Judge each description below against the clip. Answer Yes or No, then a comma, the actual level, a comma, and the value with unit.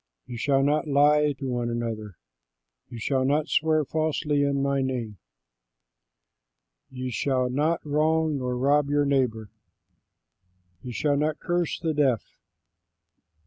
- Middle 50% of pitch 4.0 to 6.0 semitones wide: No, average, 3.0 semitones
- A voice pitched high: No, medium, 140 Hz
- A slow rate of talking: Yes, slow, 130 wpm